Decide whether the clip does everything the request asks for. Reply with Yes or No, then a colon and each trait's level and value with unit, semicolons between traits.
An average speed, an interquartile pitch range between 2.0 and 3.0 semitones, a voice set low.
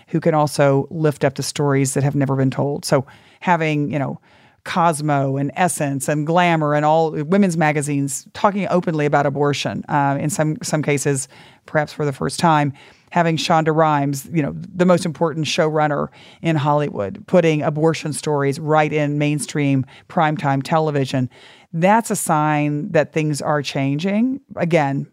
No: average, 160 wpm; narrow, 2.5 semitones; medium, 150 Hz